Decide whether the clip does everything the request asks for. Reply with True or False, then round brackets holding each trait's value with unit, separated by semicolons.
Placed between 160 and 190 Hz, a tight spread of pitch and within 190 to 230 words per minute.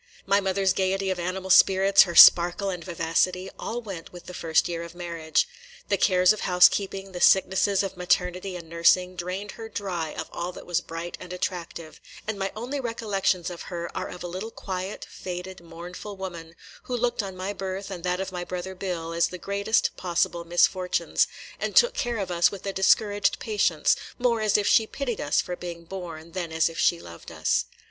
True (185 Hz; 2.2 semitones; 200 wpm)